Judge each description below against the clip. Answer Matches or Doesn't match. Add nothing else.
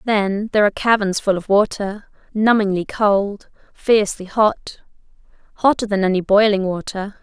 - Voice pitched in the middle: Doesn't match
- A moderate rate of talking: Doesn't match